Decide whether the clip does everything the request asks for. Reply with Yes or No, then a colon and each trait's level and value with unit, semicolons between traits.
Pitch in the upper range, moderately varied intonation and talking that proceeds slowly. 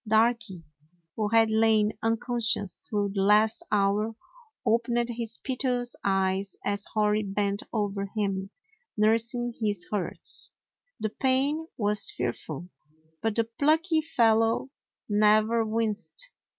No: high, 220 Hz; narrow, 2.3 semitones; slow, 110 wpm